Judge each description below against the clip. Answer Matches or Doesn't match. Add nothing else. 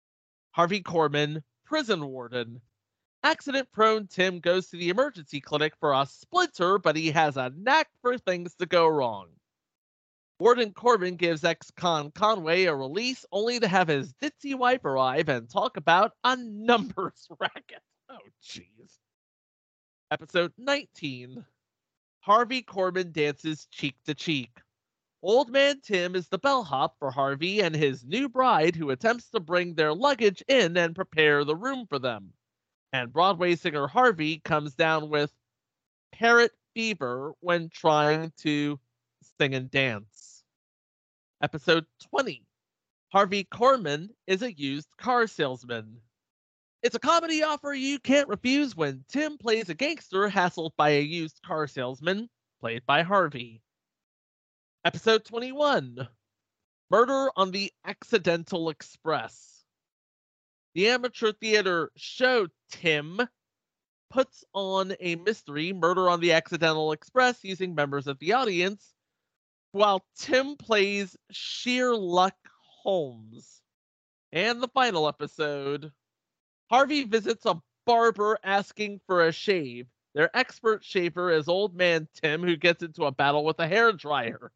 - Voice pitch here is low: Doesn't match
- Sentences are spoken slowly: Matches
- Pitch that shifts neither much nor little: Doesn't match